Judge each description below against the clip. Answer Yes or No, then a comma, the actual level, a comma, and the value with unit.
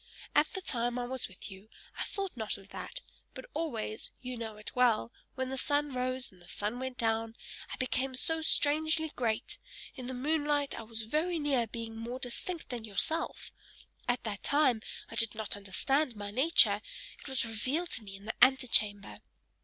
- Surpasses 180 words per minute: Yes, average, 190 wpm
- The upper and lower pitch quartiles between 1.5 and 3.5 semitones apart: No, average, 4.5 semitones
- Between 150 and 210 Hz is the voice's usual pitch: No, very high, 250 Hz